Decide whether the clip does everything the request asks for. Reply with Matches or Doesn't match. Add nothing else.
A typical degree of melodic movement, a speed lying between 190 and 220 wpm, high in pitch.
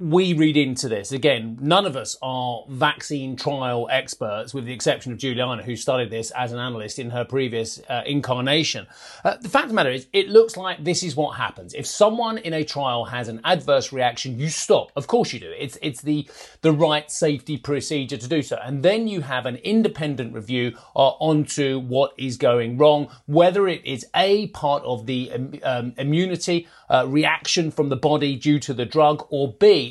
Doesn't match